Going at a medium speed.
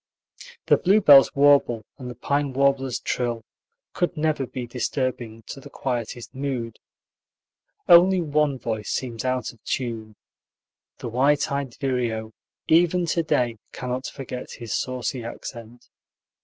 No: slow, 130 wpm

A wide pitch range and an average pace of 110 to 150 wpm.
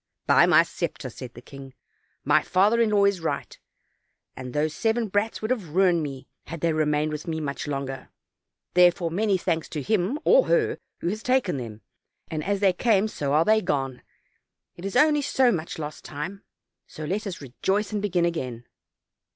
No: wide, 5.8 semitones; average, 185 wpm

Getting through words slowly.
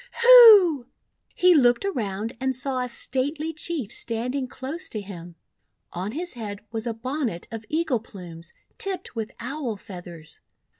No: average, 150 wpm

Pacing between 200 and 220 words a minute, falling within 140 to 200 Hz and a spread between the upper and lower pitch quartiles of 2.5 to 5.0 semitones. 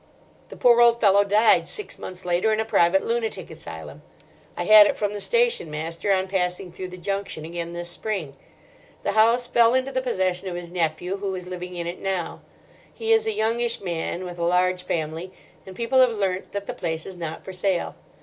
Yes: fast, 205 wpm; high, 190 Hz; average, 4.0 semitones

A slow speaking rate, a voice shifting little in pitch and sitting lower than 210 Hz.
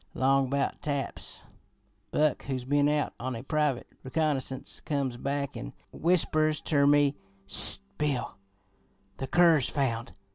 Yes: slow, 130 wpm; narrow, 2.3 semitones; medium, 140 Hz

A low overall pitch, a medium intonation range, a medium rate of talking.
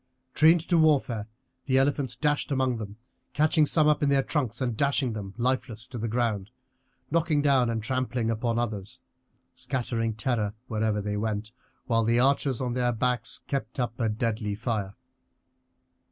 Yes: low, 120 Hz; average, 3.5 semitones; average, 160 wpm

